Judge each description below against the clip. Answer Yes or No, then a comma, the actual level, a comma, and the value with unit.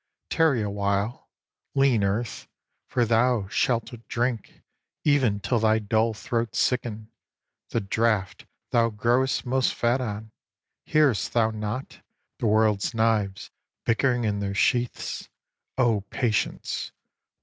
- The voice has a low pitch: Yes, low, 115 Hz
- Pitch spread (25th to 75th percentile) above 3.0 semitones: No, average, 2.7 semitones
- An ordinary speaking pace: No, slow, 115 wpm